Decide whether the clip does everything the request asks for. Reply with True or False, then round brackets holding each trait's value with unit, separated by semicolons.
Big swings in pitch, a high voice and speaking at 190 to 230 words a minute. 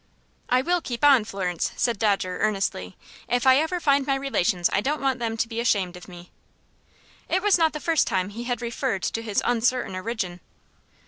True (5.7 semitones; 230 Hz; 195 wpm)